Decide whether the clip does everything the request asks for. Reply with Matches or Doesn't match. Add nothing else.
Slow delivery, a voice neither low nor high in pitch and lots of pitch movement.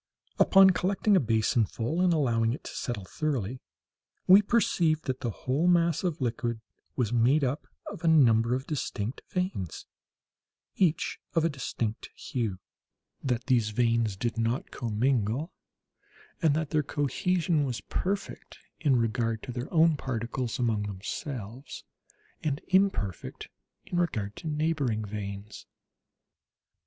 Doesn't match